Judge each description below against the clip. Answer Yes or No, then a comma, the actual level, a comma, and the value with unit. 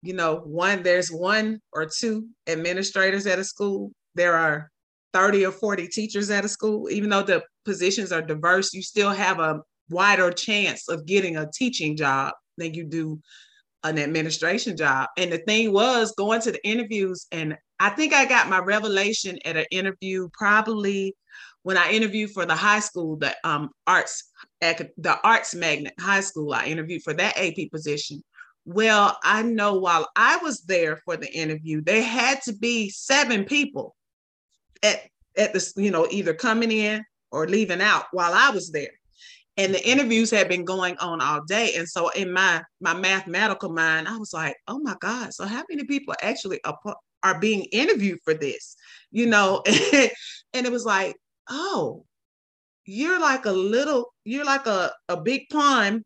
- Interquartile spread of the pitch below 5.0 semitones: Yes, average, 4.5 semitones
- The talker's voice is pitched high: Yes, high, 195 Hz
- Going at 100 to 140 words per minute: No, average, 175 wpm